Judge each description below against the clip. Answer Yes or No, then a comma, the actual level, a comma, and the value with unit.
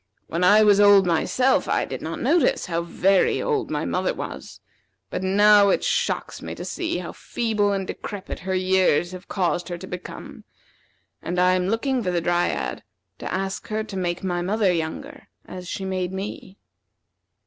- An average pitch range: No, narrow, 2.3 semitones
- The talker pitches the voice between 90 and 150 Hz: No, high, 190 Hz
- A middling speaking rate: Yes, average, 180 wpm